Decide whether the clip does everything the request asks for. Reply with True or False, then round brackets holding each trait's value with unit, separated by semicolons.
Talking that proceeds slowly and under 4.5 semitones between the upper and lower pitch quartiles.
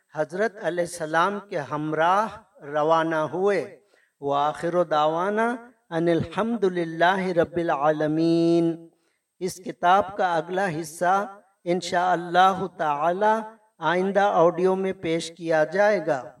True (100 wpm; 3.1 semitones)